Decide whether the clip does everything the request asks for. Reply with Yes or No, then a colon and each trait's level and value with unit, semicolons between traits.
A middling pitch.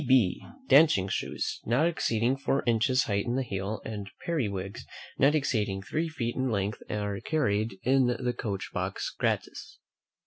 No: low, 115 Hz